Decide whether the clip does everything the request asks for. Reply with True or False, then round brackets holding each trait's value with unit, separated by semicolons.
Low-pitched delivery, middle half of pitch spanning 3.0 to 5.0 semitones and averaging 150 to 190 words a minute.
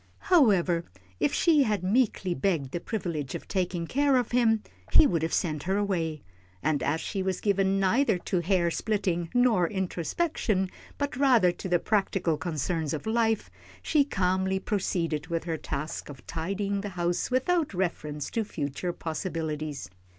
False (185 Hz; 4.5 semitones; 160 wpm)